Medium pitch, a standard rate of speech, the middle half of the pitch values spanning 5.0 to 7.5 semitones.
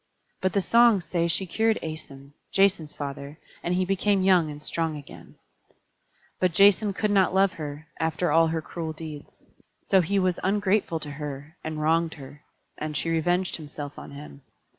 No: medium, 165 Hz; average, 170 wpm; average, 4.0 semitones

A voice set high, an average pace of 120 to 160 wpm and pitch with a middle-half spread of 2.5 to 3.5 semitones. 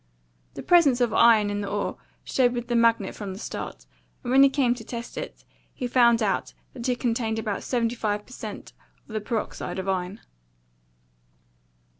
No: high, 230 Hz; average, 185 wpm; average, 2.9 semitones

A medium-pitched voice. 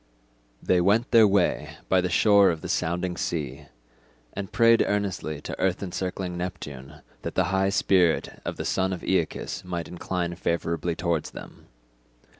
No: very low, 90 Hz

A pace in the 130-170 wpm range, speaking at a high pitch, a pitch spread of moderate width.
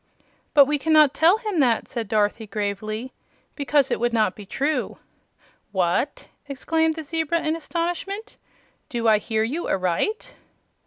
No: average, 145 wpm; very high, 275 Hz; wide, 6.9 semitones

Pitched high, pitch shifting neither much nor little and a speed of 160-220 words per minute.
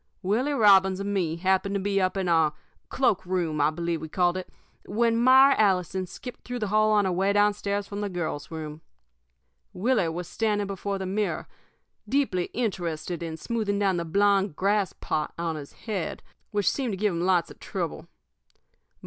Yes: high, 195 Hz; average, 3.1 semitones; average, 185 wpm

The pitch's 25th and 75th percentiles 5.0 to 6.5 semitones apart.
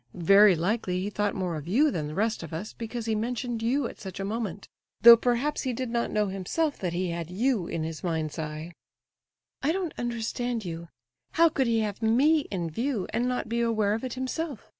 Yes: average, 5.3 semitones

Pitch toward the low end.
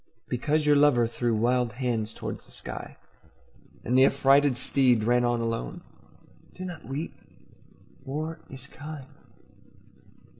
Yes: low, 130 Hz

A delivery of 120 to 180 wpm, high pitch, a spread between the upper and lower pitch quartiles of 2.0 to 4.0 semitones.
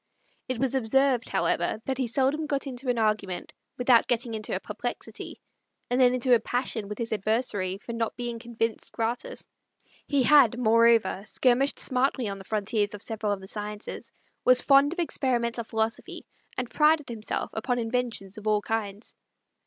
Yes: average, 170 wpm; high, 235 Hz; average, 2.9 semitones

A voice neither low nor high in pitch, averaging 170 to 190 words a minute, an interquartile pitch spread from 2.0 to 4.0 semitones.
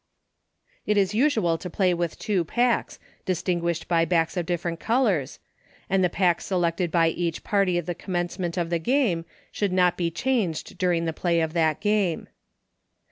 Yes: medium, 175 Hz; average, 185 wpm; narrow, 2.5 semitones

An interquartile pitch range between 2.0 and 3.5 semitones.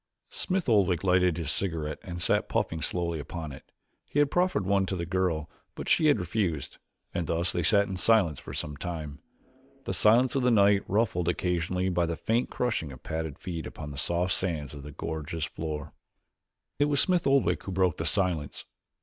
No: average, 4.2 semitones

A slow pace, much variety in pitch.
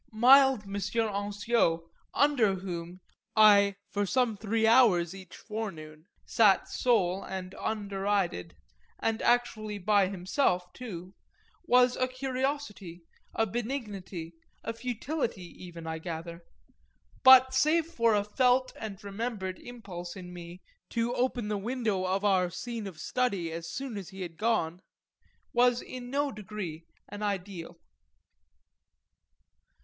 No: slow, 125 wpm; average, 4.9 semitones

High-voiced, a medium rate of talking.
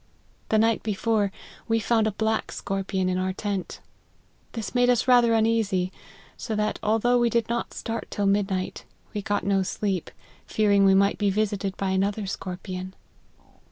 Yes: high, 205 Hz; average, 160 wpm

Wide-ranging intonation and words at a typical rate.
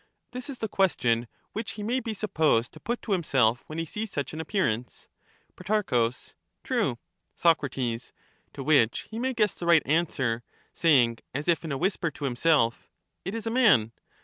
Yes: wide, 9.0 semitones; average, 180 wpm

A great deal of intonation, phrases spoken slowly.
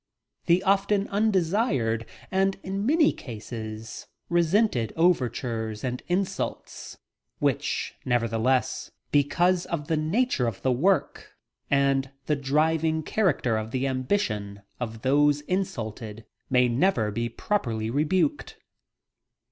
Yes: wide, 7.9 semitones; slow, 110 wpm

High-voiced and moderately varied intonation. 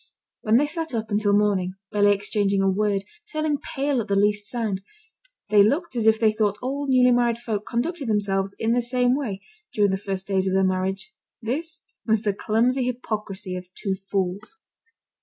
Yes: high, 215 Hz; average, 3.9 semitones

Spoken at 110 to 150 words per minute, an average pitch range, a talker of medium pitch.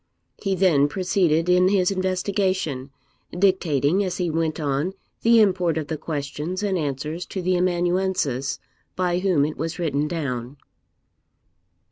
Yes: slow, 135 wpm; average, 3.8 semitones; medium, 175 Hz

